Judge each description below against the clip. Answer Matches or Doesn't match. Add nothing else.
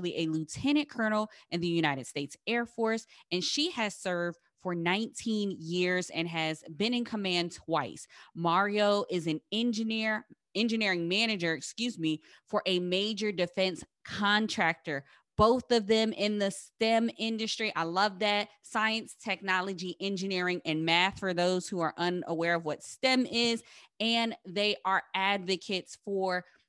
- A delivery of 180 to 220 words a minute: Doesn't match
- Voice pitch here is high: Matches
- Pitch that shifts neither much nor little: Matches